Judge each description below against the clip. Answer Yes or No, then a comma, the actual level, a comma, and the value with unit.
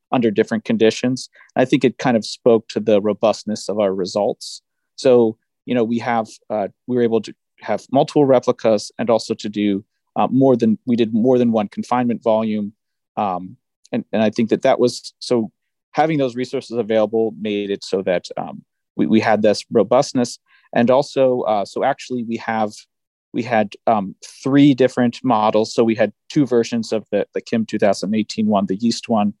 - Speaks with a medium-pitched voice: No, low, 115 Hz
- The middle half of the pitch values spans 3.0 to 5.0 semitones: No, narrow, 2.4 semitones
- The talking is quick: No, average, 190 wpm